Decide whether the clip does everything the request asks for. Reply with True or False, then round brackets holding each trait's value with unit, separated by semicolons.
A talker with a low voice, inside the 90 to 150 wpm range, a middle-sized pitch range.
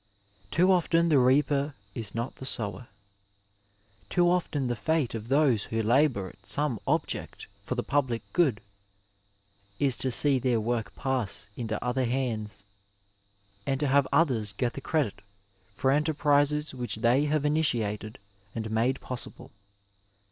True (130 Hz; 140 wpm; 4.3 semitones)